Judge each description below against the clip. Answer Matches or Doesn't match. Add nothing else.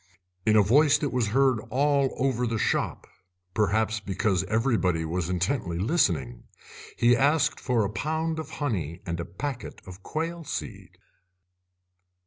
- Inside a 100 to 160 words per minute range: Matches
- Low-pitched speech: Matches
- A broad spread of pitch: Matches